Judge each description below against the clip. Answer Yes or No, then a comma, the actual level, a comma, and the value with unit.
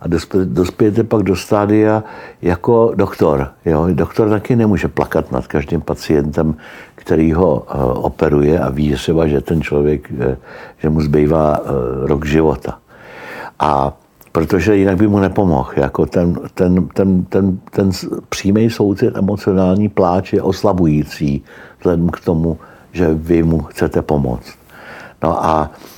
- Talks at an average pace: Yes, average, 130 wpm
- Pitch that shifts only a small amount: No, average, 4.3 semitones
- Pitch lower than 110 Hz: Yes, very low, 85 Hz